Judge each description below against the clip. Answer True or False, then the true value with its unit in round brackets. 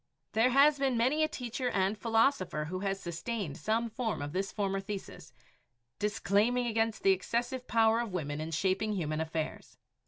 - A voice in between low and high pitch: False (215 Hz)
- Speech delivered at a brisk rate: False (165 wpm)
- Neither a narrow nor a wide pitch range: True (4.3 semitones)